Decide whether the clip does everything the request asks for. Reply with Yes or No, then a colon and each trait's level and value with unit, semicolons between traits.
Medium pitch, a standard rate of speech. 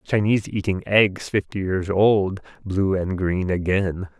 No: very low, 95 Hz; average, 145 wpm